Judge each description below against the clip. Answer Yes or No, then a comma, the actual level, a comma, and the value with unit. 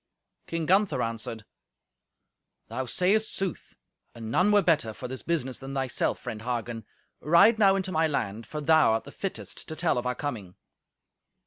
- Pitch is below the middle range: No, medium, 145 Hz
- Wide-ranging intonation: Yes, wide, 7.4 semitones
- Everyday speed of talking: Yes, average, 170 wpm